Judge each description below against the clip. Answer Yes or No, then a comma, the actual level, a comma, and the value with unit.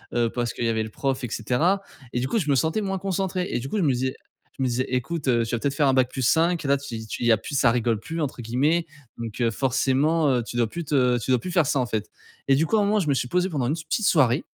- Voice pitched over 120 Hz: Yes, low, 135 Hz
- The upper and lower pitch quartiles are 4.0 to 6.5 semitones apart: Yes, average, 5.2 semitones